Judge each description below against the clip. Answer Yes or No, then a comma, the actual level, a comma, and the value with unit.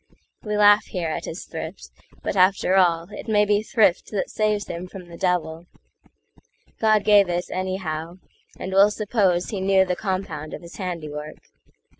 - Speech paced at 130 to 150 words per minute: Yes, average, 145 wpm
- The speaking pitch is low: No, medium, 185 Hz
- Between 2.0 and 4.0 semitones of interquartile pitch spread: Yes, average, 3.0 semitones